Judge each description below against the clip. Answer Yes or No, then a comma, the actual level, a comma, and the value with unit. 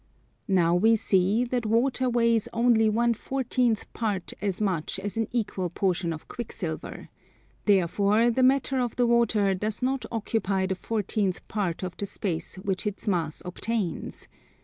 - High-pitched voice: Yes, high, 210 Hz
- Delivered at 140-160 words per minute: Yes, average, 150 wpm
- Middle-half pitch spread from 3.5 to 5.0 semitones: Yes, average, 3.8 semitones